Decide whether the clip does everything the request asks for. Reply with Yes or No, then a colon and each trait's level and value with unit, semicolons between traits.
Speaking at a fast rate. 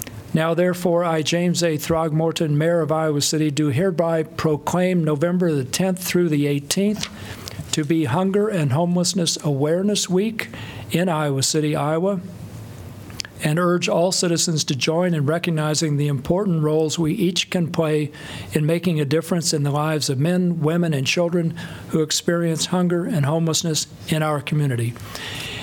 No: average, 150 wpm